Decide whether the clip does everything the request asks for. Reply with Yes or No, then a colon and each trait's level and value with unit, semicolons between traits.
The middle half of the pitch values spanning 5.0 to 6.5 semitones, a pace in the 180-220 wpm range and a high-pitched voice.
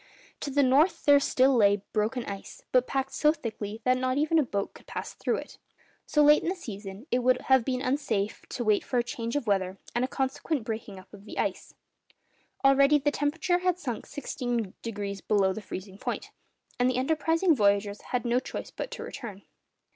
Yes: average, 5.3 semitones; average, 200 wpm; very high, 250 Hz